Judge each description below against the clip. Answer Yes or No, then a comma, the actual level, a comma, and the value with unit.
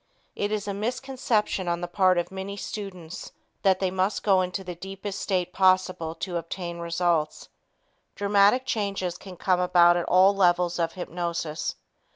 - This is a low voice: No, medium, 185 Hz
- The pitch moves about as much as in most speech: No, narrow, 2.3 semitones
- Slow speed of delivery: No, average, 160 wpm